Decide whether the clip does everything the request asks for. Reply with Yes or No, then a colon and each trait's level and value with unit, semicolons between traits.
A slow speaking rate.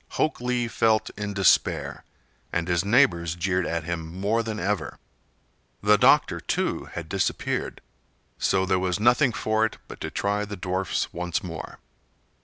No: average, 155 wpm